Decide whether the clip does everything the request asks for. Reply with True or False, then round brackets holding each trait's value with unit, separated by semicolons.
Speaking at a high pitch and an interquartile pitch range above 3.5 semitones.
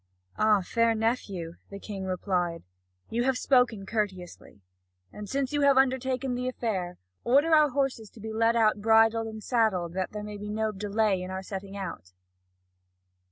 True (220 Hz; 4.1 semitones)